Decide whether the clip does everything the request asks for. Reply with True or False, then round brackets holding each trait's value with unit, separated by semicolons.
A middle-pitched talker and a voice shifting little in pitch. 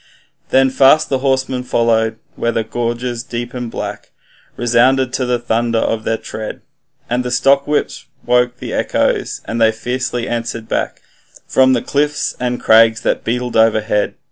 False (120 Hz; 2.1 semitones)